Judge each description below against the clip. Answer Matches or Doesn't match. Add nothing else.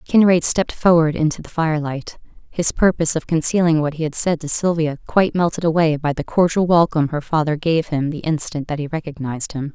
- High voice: Doesn't match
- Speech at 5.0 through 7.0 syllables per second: Matches